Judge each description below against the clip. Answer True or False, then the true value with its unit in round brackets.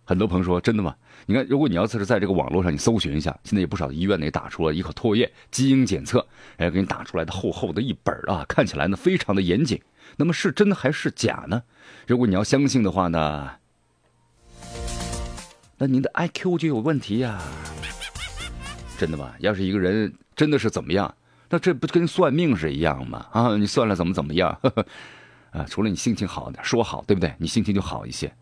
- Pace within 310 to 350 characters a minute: True (320 characters per minute)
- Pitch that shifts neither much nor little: False (7.4 semitones)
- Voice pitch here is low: True (105 Hz)